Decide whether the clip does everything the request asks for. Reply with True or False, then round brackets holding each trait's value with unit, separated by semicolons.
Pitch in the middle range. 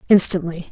True (175 Hz)